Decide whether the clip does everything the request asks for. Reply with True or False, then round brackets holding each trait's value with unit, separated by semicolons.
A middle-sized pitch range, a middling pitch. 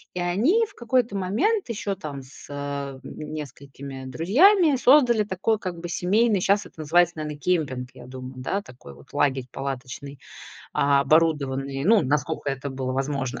False (6.7 semitones; 150 Hz)